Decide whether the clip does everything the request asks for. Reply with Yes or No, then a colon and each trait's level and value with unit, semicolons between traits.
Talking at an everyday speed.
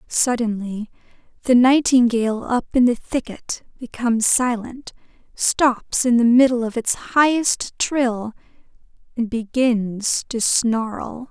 No: slow, 110 wpm